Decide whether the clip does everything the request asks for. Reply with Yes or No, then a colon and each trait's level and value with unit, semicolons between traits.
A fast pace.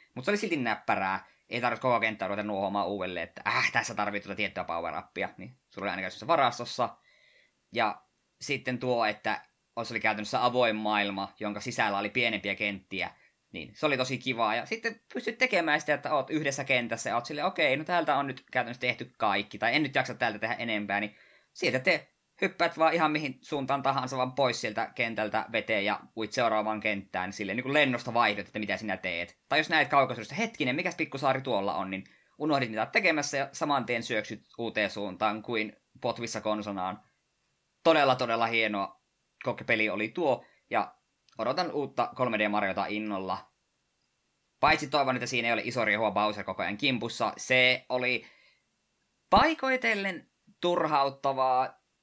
Yes: fast, 170 wpm